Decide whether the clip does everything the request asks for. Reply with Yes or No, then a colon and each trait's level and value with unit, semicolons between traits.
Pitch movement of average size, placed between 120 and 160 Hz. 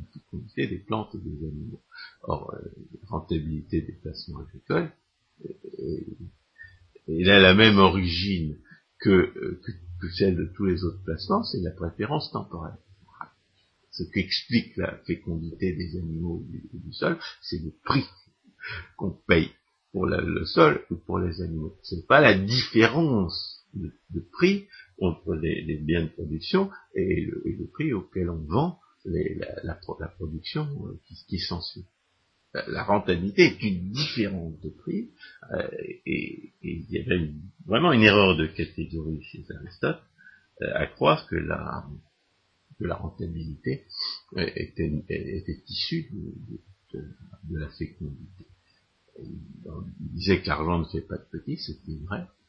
No: average, 4.5 semitones; very low, 90 Hz